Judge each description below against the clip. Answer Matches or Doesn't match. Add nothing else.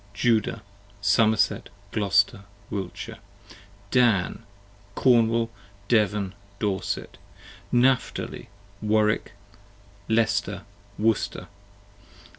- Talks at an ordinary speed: Doesn't match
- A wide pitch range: Doesn't match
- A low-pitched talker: Matches